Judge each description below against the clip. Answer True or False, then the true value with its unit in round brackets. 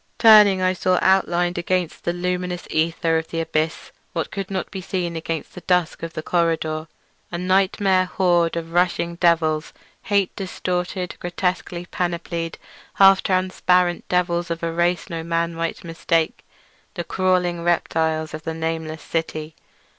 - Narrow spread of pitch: True (1.8 semitones)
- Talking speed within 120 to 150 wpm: True (140 wpm)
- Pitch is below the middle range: False (175 Hz)